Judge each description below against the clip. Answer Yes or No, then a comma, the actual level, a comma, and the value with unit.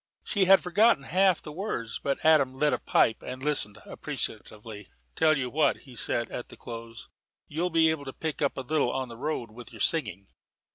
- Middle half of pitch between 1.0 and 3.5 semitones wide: No, average, 5.2 semitones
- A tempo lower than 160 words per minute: No, average, 200 wpm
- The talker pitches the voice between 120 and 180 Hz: Yes, medium, 140 Hz